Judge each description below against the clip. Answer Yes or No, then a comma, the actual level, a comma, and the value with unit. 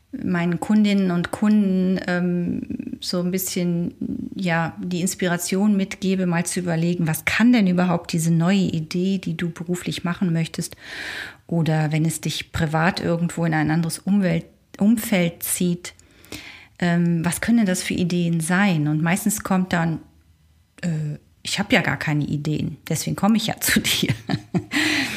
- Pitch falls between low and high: Yes, medium, 175 Hz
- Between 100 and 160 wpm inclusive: Yes, average, 155 wpm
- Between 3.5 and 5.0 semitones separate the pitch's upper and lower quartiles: No, average, 2.7 semitones